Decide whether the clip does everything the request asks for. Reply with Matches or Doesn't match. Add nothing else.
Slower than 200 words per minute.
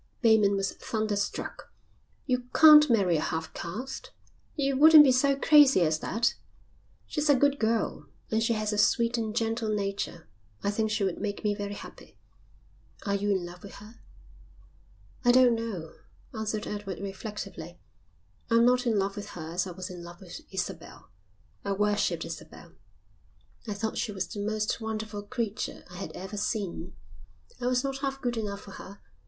Matches